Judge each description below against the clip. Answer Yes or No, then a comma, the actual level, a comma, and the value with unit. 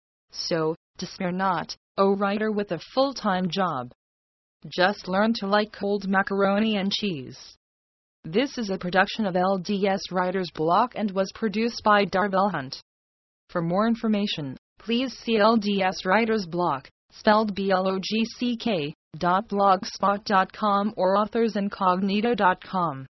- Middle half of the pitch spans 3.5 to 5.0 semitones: No, average, 3.0 semitones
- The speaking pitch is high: Yes, high, 195 Hz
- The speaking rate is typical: No, slow, 115 wpm